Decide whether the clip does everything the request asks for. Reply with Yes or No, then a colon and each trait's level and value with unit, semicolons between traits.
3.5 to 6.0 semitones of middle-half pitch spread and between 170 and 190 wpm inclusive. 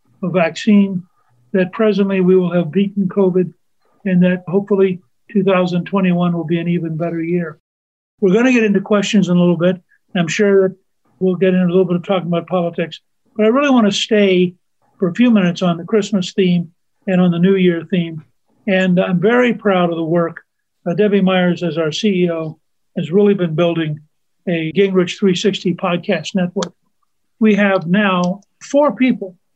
No: narrow, 2.4 semitones; average, 180 wpm